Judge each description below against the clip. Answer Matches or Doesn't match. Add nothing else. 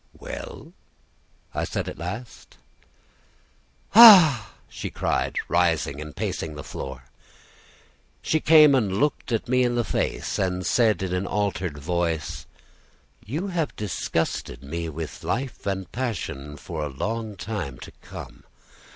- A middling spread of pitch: Doesn't match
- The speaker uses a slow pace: Matches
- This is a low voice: Matches